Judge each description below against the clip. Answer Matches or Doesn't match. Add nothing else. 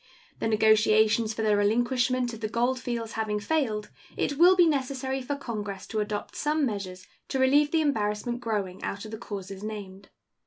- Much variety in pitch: Doesn't match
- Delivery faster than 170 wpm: Matches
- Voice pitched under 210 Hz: Doesn't match